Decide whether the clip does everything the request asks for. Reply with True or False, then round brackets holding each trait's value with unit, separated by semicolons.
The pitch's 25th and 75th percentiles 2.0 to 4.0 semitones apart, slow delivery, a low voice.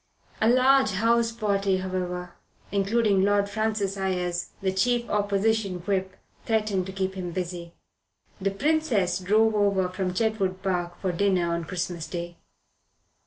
False (2.9 semitones; 130 wpm; 195 Hz)